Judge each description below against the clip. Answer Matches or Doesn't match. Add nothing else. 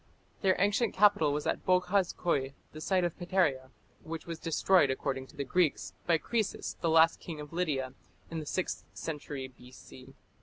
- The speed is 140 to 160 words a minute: Doesn't match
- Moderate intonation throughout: Matches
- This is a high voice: Doesn't match